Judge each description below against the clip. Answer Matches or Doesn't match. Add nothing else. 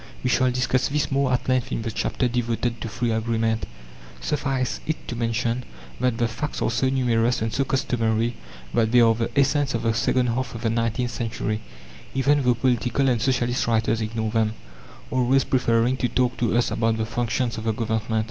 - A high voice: Doesn't match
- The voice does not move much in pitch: Matches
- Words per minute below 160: Doesn't match